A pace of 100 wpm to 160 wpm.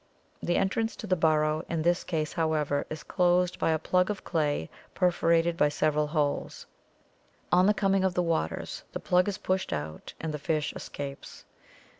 No: average, 175 wpm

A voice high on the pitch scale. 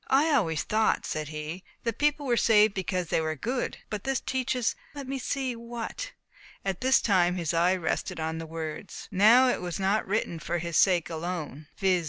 Yes: high, 195 Hz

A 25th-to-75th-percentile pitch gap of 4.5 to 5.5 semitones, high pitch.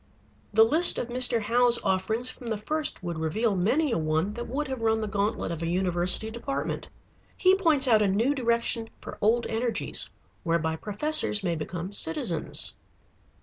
Yes: average, 5.0 semitones; high, 220 Hz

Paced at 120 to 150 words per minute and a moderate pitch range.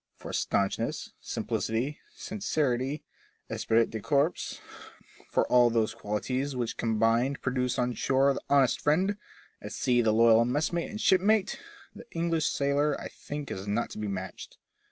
Yes: average, 145 wpm; average, 4.5 semitones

